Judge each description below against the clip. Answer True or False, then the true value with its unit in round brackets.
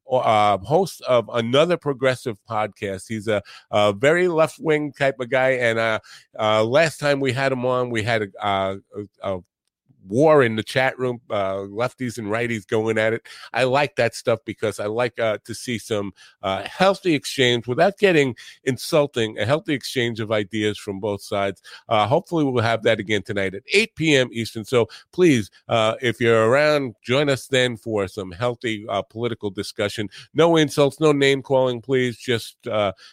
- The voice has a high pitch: False (120 Hz)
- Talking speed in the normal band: True (185 wpm)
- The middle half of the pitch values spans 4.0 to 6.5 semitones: True (4.3 semitones)